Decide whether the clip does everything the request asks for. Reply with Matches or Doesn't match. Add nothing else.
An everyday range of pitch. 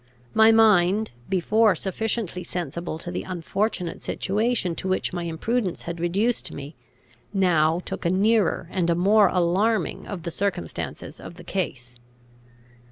Matches